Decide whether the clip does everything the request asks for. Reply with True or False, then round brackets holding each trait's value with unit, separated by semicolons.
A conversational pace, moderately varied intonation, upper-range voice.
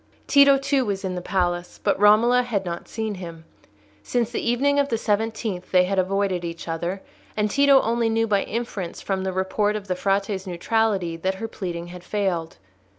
True (190 wpm; 3.8 semitones; 200 Hz)